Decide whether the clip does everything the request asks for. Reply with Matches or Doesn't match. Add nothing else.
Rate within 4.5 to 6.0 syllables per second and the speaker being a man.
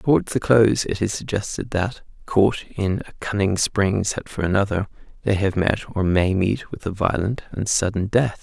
Matches